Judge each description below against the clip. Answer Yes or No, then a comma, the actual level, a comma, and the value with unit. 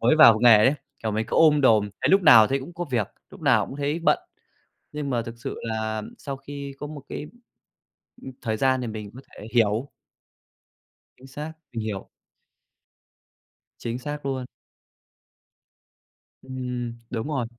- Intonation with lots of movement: No, average, 4.1 semitones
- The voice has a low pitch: Yes, low, 125 Hz